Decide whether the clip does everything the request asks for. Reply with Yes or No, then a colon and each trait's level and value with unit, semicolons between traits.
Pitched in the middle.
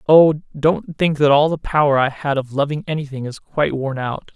Yes: medium, 145 Hz